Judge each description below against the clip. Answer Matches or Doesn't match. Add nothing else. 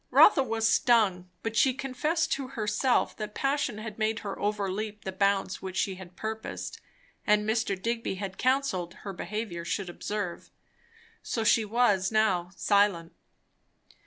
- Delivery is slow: Doesn't match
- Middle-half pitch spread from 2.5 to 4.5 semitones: Matches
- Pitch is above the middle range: Matches